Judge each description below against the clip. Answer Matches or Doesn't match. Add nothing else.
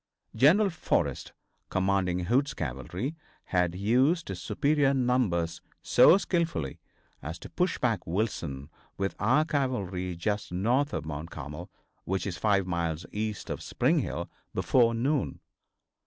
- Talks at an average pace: Doesn't match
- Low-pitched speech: Matches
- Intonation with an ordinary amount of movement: Doesn't match